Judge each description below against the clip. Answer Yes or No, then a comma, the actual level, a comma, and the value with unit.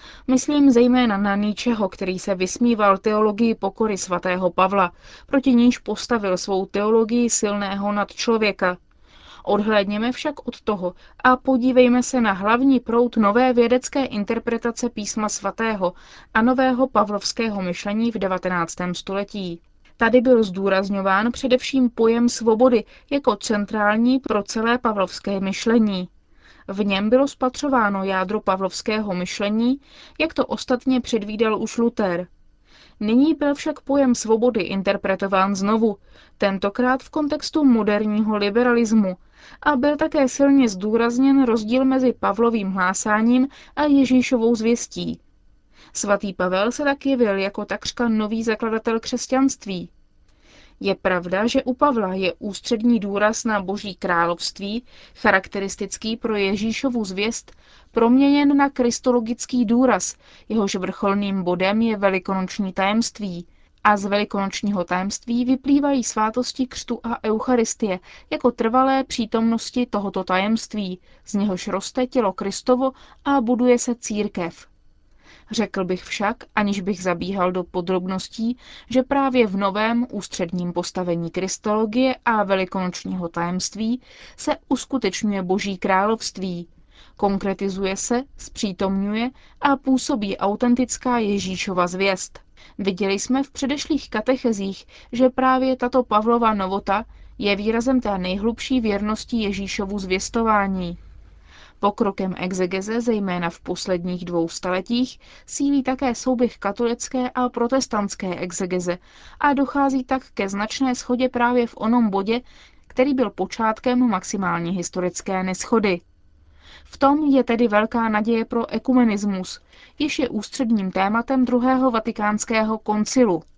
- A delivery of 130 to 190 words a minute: No, slow, 115 wpm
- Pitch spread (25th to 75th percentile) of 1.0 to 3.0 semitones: No, average, 4.2 semitones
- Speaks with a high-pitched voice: Yes, high, 220 Hz